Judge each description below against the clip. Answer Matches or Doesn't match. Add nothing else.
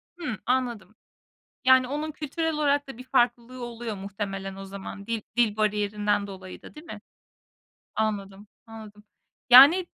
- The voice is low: Doesn't match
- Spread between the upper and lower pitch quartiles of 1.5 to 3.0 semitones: Doesn't match